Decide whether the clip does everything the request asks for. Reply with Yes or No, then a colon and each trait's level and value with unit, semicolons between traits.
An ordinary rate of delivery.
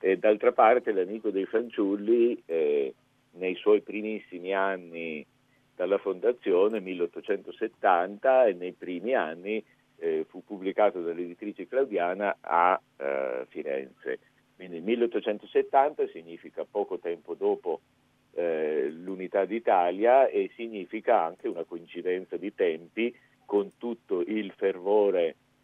No: slow, 110 wpm